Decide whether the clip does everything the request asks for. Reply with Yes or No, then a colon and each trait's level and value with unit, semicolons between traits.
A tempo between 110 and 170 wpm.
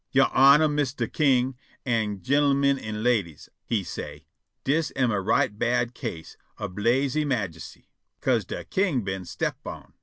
Yes: average, 150 wpm